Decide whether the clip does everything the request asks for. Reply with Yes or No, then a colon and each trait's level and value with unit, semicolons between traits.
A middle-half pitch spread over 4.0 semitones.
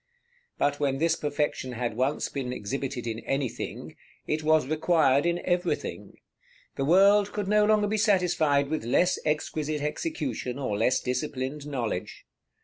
Yes: average, 4.8 semitones